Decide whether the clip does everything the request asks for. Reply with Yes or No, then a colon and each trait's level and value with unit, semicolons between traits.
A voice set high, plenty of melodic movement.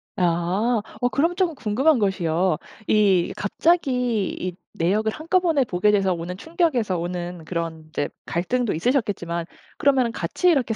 Yes: high, 210 Hz; wide, 6.9 semitones